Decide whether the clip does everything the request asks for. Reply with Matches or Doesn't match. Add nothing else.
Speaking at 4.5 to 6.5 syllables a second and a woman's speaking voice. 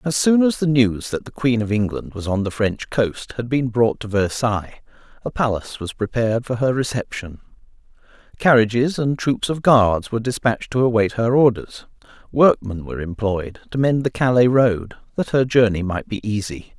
Doesn't match